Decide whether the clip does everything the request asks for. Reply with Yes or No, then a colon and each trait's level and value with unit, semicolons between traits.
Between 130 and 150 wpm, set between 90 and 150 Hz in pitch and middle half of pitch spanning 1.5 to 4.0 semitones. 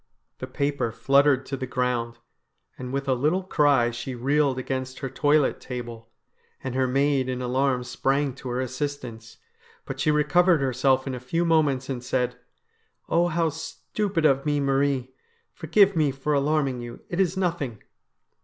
No: average, 165 wpm; low, 135 Hz; average, 2.8 semitones